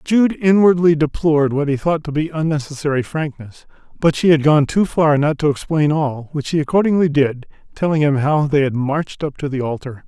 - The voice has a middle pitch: Yes, medium, 150 Hz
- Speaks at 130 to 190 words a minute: No, fast, 205 wpm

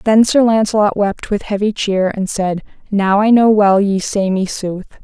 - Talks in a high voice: Yes, high, 205 Hz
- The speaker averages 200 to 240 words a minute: Yes, fast, 205 wpm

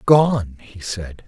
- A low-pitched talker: Yes, low, 110 Hz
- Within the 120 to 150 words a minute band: Yes, average, 140 wpm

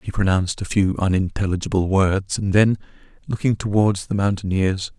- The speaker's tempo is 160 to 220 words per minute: No, average, 145 wpm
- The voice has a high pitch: No, low, 100 Hz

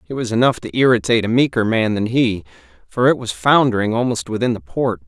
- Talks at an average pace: No, fast, 215 wpm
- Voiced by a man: Yes, male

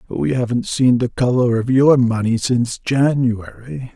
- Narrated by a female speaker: No, male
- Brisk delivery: No, average, 150 wpm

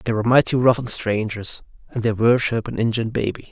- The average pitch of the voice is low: Yes, low, 115 Hz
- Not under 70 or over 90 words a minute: No, fast, 205 wpm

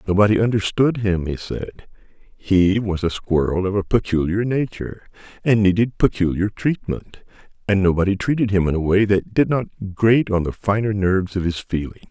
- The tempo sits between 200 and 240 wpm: No, average, 170 wpm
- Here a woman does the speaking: No, male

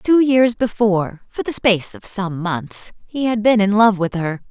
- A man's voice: No, female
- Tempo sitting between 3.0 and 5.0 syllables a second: Yes, 4.5 syllables/s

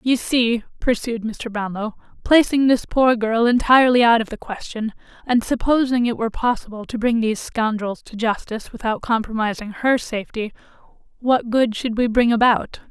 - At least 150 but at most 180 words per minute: Yes, average, 165 wpm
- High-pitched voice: Yes, high, 230 Hz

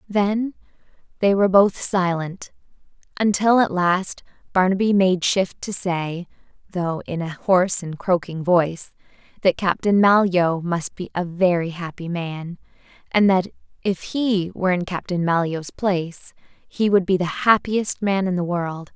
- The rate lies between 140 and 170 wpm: Yes, average, 150 wpm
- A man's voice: No, female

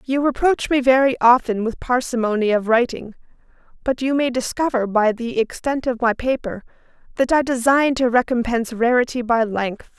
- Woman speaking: Yes, female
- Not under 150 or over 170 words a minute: Yes, average, 160 wpm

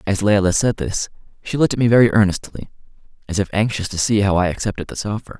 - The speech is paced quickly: Yes, fast, 220 wpm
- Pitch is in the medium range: No, low, 100 Hz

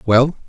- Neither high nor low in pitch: No, low, 130 Hz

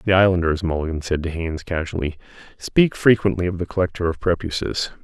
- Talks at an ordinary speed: Yes, average, 165 wpm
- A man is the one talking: Yes, male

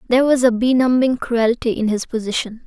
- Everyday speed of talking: Yes, average, 180 wpm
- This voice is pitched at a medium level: No, high, 240 Hz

